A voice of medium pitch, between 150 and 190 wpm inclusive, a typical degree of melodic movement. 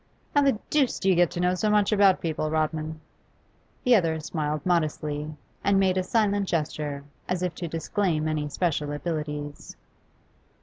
Yes: medium, 165 Hz; average, 165 wpm; average, 3.9 semitones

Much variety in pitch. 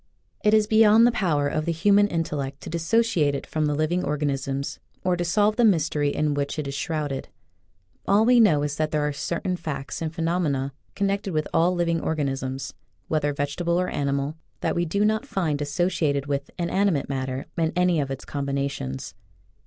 No: average, 4.2 semitones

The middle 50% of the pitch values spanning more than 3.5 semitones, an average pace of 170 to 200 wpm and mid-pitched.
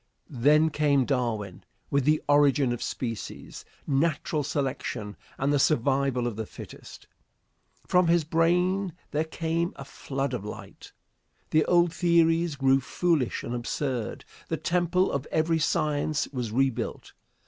No: average, 4.0 semitones; slow, 135 wpm; medium, 145 Hz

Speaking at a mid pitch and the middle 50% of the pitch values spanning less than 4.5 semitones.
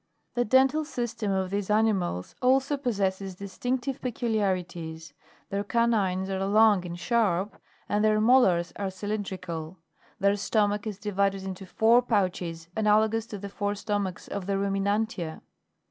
No: high, 205 Hz; average, 2.8 semitones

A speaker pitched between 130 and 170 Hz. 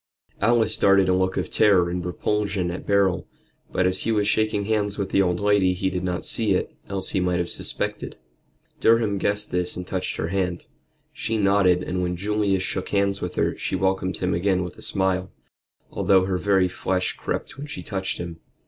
No: very low, 95 Hz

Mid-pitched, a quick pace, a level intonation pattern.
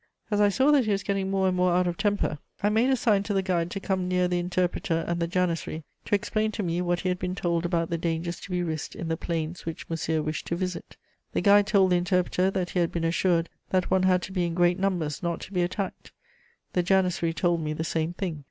Yes: medium, 180 Hz; fast, 260 wpm; narrow, 2.2 semitones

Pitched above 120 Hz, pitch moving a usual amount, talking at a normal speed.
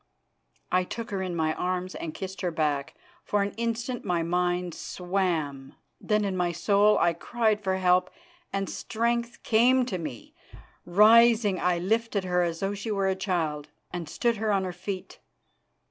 Yes: high, 190 Hz; average, 3.3 semitones; average, 170 wpm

